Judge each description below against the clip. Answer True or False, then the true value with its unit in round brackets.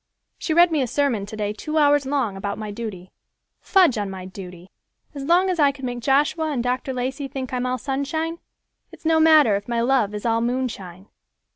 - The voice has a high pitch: True (255 Hz)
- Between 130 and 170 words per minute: False (205 wpm)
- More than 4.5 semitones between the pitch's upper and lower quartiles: True (5.6 semitones)